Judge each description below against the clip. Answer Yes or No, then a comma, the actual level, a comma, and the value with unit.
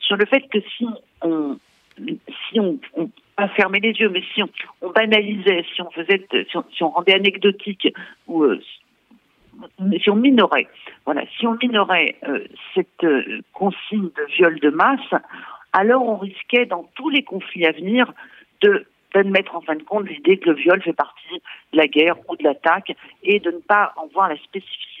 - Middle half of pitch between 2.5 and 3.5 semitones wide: No, average, 4.2 semitones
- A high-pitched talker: Yes, high, 195 Hz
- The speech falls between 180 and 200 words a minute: Yes, average, 190 wpm